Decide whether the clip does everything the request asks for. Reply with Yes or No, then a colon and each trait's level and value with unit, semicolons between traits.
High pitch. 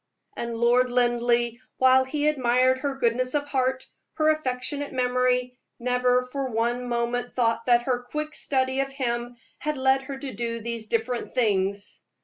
Yes: very high, 250 Hz